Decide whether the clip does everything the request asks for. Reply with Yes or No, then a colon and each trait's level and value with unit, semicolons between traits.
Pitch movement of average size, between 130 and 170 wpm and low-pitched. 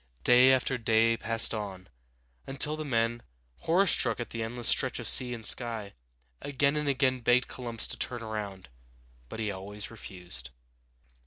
Yes: average, 3.2 semitones; average, 160 wpm; low, 115 Hz